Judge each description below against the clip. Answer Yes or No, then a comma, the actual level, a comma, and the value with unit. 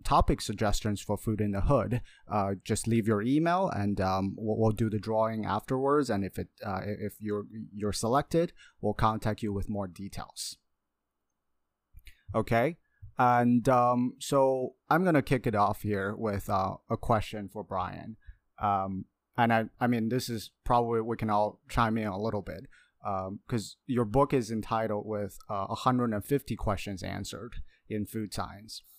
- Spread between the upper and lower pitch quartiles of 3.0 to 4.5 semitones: Yes, average, 3.3 semitones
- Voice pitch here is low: Yes, low, 110 Hz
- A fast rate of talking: No, average, 170 wpm